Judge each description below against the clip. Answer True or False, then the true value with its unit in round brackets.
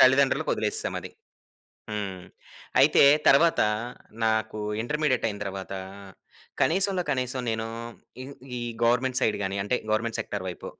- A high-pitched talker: False (115 Hz)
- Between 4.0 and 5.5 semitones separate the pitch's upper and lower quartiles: True (4.3 semitones)